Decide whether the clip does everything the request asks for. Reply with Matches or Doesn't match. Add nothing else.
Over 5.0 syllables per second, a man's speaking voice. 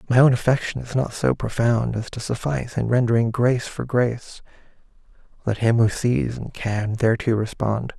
Matches